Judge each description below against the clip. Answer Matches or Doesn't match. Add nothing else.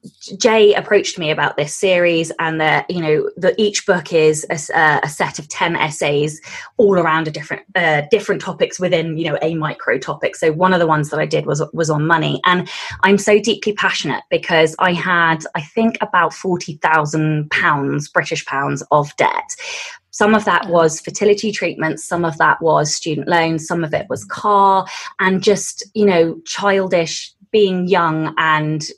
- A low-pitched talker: Doesn't match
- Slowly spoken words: Doesn't match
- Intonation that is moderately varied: Matches